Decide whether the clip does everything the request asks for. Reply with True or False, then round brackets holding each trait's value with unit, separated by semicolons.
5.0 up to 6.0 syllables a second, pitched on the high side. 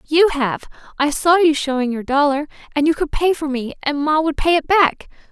True (5.2 syllables/s; 300 Hz)